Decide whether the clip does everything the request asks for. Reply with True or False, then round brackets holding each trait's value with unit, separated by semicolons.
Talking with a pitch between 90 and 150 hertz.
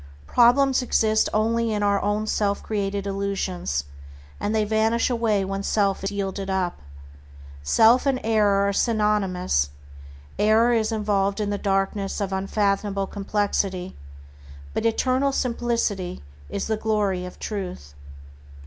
False (205 Hz)